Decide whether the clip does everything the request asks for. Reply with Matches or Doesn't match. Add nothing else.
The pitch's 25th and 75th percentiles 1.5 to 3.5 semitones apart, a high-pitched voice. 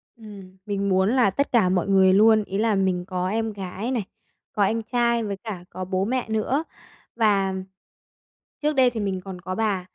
Matches